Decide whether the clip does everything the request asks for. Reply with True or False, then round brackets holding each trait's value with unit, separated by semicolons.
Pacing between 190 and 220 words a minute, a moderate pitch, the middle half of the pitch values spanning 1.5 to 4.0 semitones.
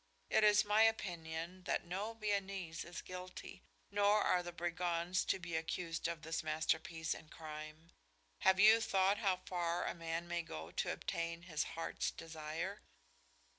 False (155 wpm; 175 Hz; 2.8 semitones)